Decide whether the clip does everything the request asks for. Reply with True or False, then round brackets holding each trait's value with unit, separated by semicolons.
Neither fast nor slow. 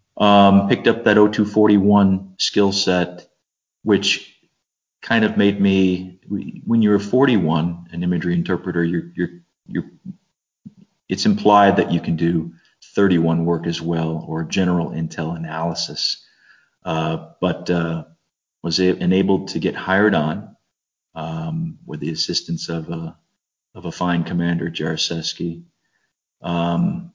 False (125 wpm)